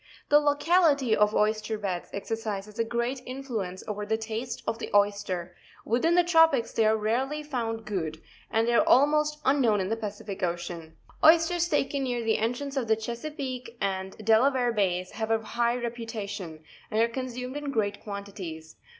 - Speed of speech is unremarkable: Yes, average, 170 wpm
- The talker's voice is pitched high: Yes, high, 225 Hz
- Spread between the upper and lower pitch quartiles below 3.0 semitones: No, average, 4.3 semitones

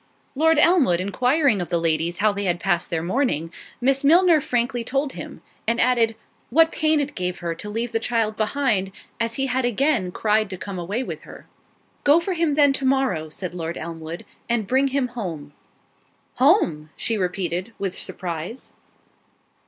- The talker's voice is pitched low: No, high, 225 Hz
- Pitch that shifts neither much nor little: No, wide, 7.2 semitones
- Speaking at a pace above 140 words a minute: Yes, average, 175 wpm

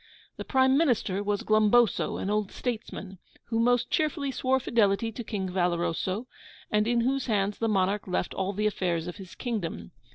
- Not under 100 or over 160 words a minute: No, average, 170 wpm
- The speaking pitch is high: Yes, high, 210 Hz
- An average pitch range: Yes, average, 4.0 semitones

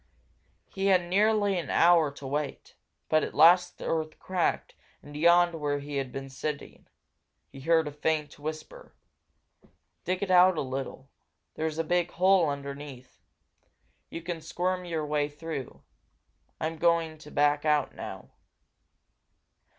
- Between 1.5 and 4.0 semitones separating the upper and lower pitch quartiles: Yes, average, 3.2 semitones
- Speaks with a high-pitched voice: No, medium, 160 Hz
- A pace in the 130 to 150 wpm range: Yes, average, 145 wpm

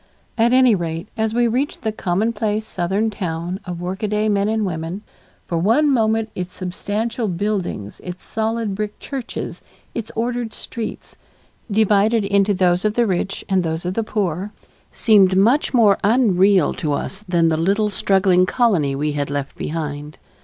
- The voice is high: Yes, high, 200 Hz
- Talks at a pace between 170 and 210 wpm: No, average, 160 wpm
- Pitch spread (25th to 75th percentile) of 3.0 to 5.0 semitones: Yes, average, 3.9 semitones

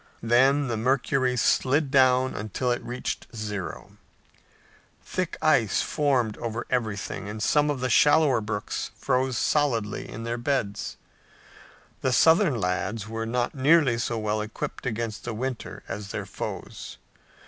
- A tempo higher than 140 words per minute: No, slow, 135 wpm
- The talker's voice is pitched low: Yes, low, 120 Hz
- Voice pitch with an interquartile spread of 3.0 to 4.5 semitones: Yes, average, 3.5 semitones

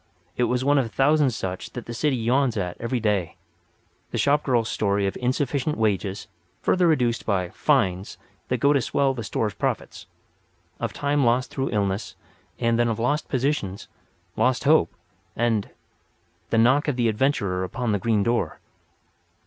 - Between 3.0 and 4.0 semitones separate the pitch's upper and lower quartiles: No, average, 4.4 semitones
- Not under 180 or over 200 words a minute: No, average, 160 wpm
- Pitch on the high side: No, low, 120 Hz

